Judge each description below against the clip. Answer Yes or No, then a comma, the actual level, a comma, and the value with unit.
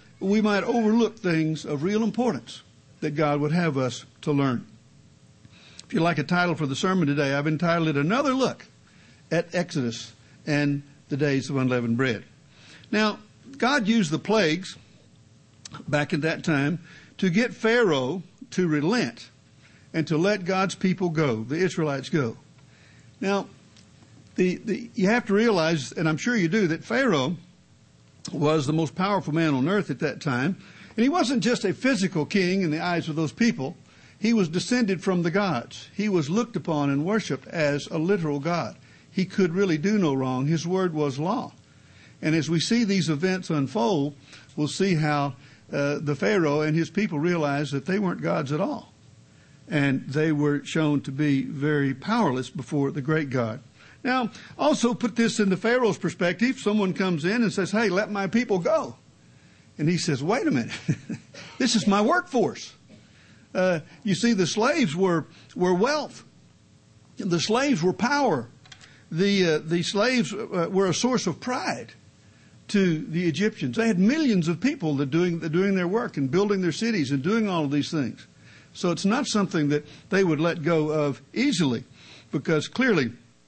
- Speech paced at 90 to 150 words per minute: No, average, 175 wpm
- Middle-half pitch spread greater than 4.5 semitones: Yes, wide, 5.6 semitones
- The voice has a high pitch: No, medium, 170 Hz